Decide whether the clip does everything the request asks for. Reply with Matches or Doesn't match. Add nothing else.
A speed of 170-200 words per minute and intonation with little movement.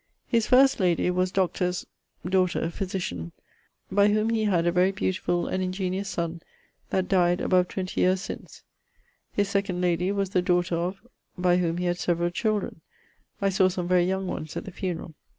Matches